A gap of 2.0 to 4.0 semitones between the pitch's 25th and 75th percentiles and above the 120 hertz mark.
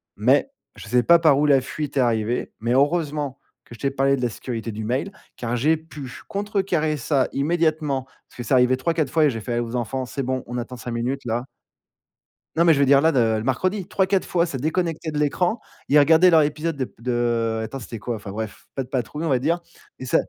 No: average, 4.7 semitones; low, 135 Hz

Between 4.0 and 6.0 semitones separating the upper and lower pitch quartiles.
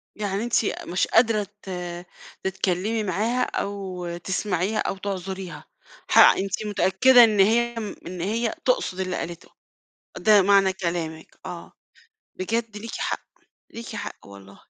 No: average, 3.3 semitones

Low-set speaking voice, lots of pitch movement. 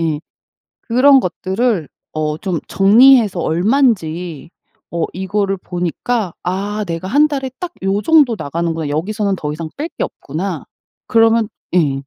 No: high, 190 Hz; wide, 5.7 semitones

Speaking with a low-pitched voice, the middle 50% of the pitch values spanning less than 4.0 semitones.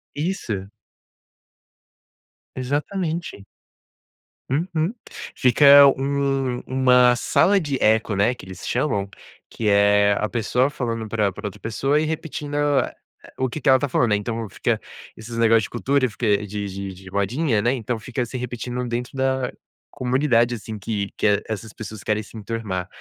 No: low, 120 Hz; average, 4.4 semitones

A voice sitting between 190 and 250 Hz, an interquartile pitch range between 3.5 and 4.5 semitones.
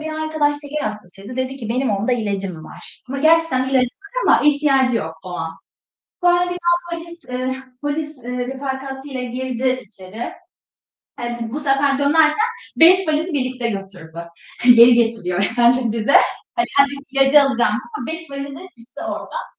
No: very high, 260 Hz; average, 4.1 semitones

